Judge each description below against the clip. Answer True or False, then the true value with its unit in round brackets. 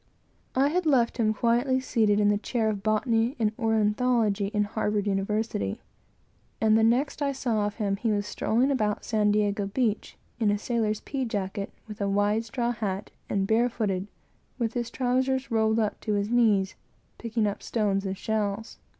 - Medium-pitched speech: False (220 Hz)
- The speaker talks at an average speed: True (170 wpm)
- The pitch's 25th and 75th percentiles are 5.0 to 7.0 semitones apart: False (2.5 semitones)